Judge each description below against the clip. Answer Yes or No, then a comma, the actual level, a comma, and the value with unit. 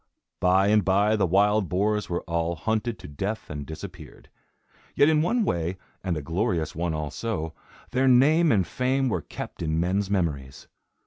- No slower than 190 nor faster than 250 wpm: No, average, 170 wpm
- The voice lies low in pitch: Yes, very low, 95 Hz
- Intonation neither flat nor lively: Yes, average, 4.9 semitones